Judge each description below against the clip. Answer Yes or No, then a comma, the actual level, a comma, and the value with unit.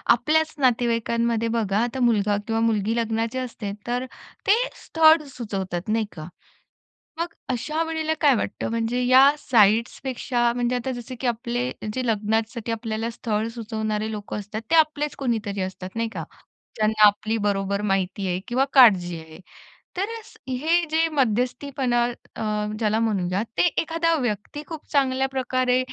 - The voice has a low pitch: No, high, 230 Hz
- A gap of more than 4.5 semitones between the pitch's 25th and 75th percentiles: No, average, 3.4 semitones